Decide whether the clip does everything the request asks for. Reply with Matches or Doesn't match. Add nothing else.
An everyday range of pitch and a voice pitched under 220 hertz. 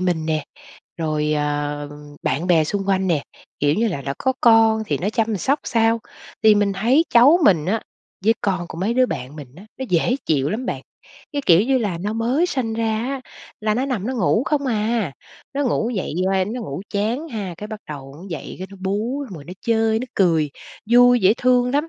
Doesn't match